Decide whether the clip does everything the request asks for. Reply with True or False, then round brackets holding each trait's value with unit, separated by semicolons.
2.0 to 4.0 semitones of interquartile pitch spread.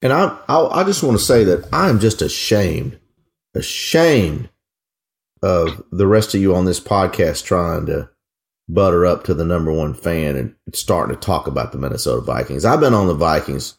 False (4.7 semitones)